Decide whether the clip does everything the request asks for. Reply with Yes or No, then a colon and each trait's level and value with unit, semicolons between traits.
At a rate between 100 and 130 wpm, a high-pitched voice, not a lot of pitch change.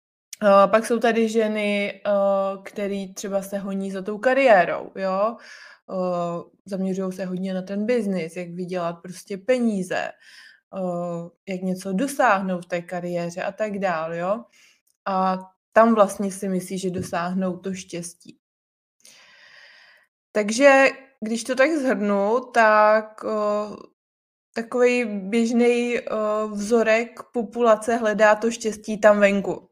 No: slow, 115 wpm; high, 200 Hz; average, 3.2 semitones